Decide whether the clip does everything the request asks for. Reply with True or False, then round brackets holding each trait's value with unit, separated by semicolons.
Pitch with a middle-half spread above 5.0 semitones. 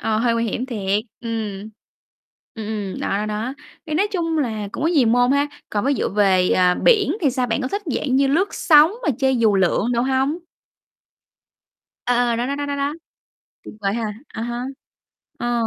False (4.7 semitones)